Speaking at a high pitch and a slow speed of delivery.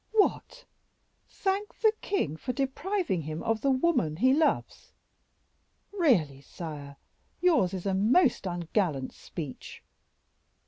Yes: high, 220 Hz; slow, 110 wpm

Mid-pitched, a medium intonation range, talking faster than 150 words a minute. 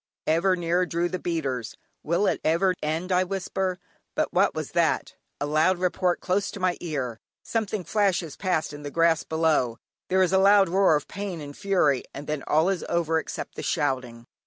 Yes: medium, 170 Hz; average, 3.6 semitones; average, 190 wpm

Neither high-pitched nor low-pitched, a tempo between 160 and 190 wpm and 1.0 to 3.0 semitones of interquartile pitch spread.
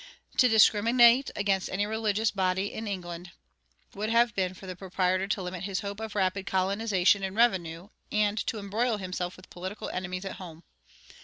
No: high, 195 Hz; average, 170 wpm; narrow, 2.5 semitones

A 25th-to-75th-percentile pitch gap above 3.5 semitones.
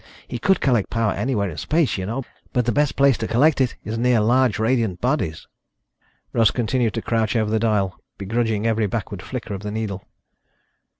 No: average, 3.0 semitones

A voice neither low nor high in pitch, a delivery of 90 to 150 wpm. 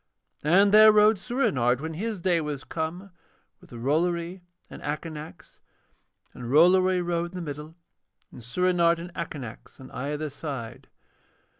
Yes: medium, 165 Hz; slow, 135 wpm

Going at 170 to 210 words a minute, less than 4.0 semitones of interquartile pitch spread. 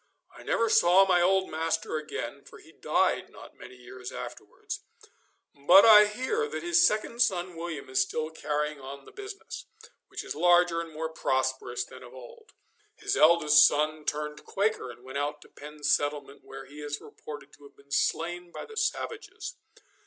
No: average, 175 wpm; average, 4.4 semitones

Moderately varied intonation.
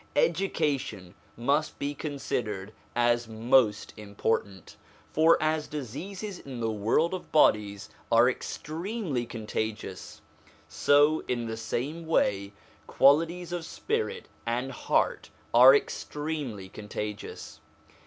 No: wide, 6.2 semitones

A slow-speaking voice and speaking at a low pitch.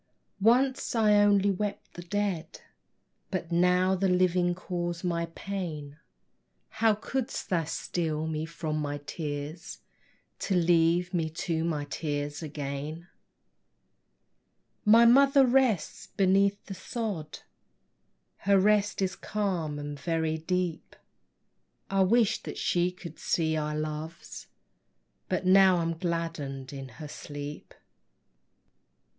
No: slow, 115 wpm; medium, 175 Hz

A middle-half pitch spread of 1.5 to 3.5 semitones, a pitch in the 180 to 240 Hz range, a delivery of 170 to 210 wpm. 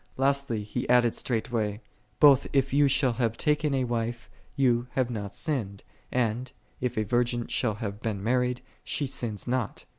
No: average, 2.7 semitones; low, 120 Hz; average, 175 wpm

